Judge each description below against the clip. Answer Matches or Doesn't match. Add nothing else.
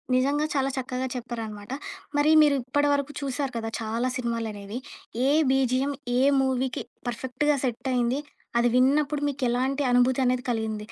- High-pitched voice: Matches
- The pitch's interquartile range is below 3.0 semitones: Matches